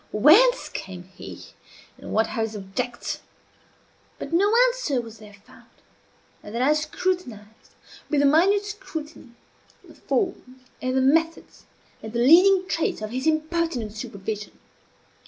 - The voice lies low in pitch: No, very high, 265 Hz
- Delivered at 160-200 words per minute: No, average, 140 wpm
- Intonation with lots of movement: Yes, wide, 7.2 semitones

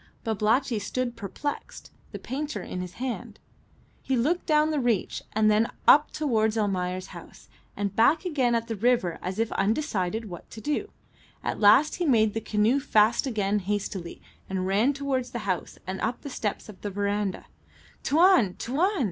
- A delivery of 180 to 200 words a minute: No, average, 165 wpm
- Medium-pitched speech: No, high, 225 Hz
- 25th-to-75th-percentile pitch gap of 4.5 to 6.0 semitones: Yes, average, 4.9 semitones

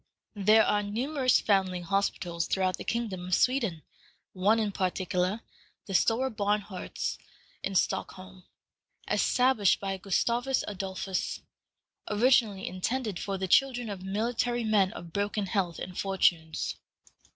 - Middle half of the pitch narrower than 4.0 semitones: Yes, average, 3.3 semitones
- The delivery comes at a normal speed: No, slow, 120 wpm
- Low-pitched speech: No, high, 200 Hz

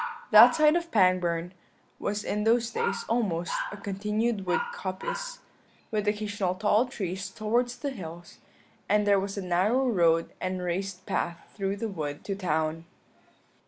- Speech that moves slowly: No, average, 155 wpm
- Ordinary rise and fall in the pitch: Yes, average, 3.8 semitones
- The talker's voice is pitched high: Yes, high, 200 Hz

